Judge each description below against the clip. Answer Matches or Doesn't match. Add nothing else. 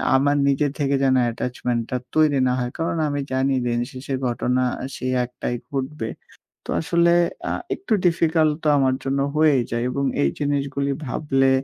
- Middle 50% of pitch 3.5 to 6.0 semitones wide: Doesn't match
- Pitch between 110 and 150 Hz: Matches